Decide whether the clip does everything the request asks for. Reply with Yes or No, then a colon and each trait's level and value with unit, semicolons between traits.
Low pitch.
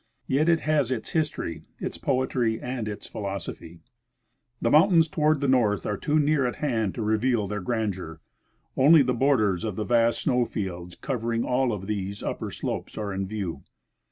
Yes: low, 115 Hz